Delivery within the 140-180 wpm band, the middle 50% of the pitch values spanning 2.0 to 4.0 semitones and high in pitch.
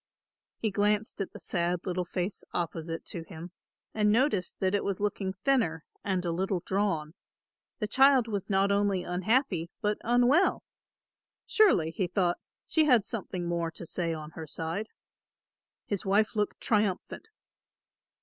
Yes: average, 150 wpm; average, 3.6 semitones; high, 195 Hz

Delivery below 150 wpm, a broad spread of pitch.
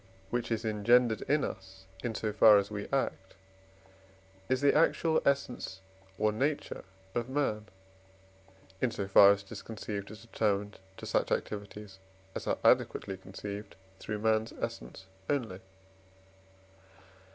No: average, 140 wpm; average, 3.3 semitones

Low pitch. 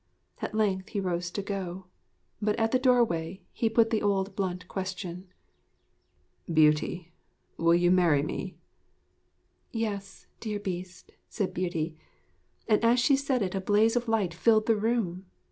No: high, 195 Hz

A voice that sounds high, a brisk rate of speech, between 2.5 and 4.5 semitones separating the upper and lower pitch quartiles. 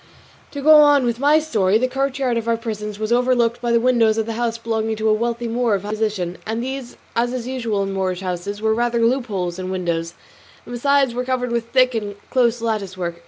Yes: high, 230 Hz; fast, 225 wpm; average, 2.9 semitones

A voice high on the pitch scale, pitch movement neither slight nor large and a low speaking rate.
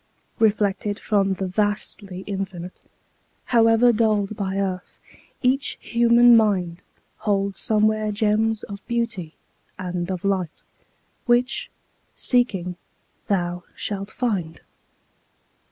Yes: high, 205 Hz; average, 3.0 semitones; slow, 95 wpm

